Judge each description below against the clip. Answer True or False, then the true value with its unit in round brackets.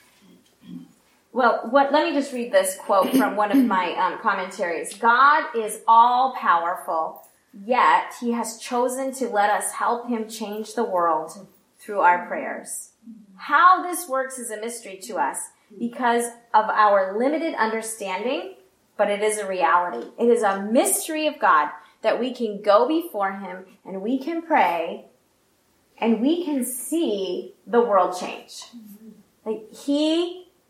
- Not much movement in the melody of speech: False (5.2 semitones)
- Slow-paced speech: False (145 wpm)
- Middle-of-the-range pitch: False (235 Hz)